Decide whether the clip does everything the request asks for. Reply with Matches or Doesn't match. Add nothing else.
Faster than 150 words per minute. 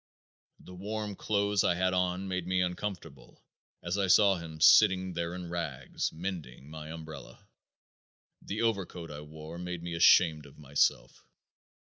Doesn't match